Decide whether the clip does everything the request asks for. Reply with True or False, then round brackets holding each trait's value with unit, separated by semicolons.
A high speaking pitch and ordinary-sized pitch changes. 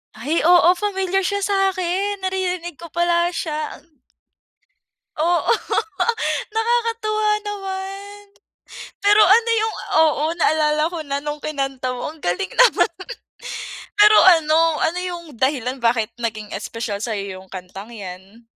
False (335 Hz; 7.4 semitones)